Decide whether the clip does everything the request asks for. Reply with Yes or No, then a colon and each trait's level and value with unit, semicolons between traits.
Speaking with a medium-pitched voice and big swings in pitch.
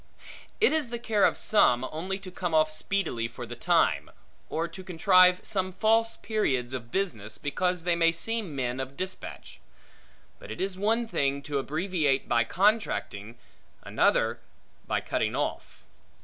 Yes: medium, 175 Hz; wide, 6.6 semitones